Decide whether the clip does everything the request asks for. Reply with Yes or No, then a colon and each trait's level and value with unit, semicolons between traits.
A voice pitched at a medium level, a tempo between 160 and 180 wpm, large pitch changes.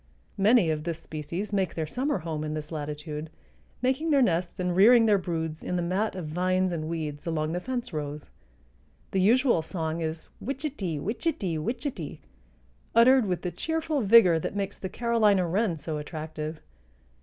Yes: medium, 180 Hz; average, 165 wpm; wide, 6.2 semitones